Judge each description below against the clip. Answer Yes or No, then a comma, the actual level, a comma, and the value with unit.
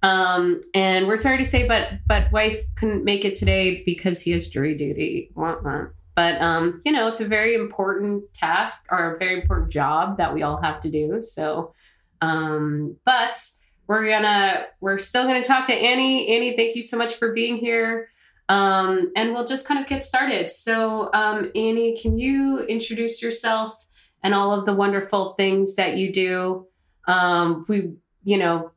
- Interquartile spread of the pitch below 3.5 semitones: No, average, 4.0 semitones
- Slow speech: No, average, 180 wpm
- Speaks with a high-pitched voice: Yes, high, 200 Hz